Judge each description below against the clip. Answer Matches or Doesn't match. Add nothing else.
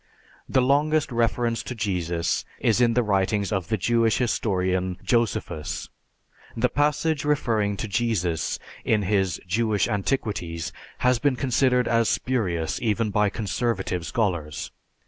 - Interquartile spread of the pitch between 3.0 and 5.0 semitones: Matches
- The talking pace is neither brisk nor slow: Doesn't match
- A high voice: Doesn't match